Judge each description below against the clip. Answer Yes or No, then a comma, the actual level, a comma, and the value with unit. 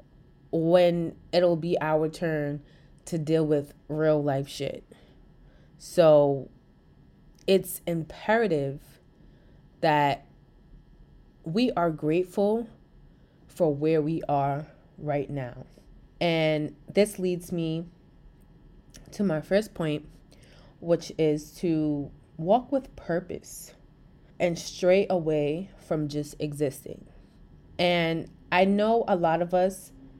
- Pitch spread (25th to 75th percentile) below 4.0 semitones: Yes, average, 3.1 semitones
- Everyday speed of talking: No, slow, 100 wpm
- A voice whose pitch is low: No, medium, 160 Hz